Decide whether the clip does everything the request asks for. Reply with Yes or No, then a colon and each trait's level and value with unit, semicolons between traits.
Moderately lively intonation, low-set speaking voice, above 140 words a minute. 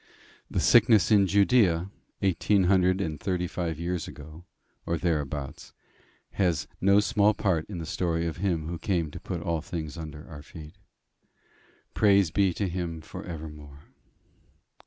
Yes: average, 3.4 semitones; very low, 85 Hz; average, 150 wpm